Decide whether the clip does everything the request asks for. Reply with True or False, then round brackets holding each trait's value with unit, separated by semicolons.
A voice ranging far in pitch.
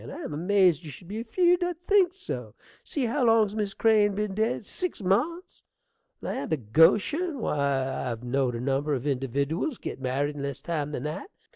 True (8.9 semitones)